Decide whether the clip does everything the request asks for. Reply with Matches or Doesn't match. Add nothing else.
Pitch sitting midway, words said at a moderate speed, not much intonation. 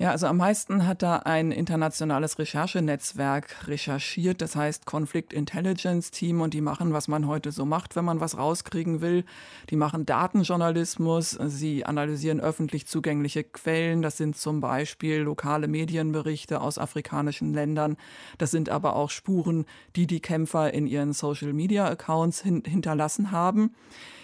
Matches